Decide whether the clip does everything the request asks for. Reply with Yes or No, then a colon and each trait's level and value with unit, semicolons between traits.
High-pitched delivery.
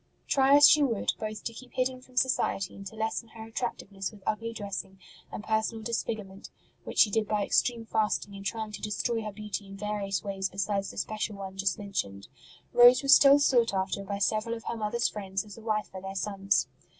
Yes: high, 210 Hz